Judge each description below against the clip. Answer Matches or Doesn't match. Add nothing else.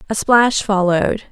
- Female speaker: Matches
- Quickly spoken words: Doesn't match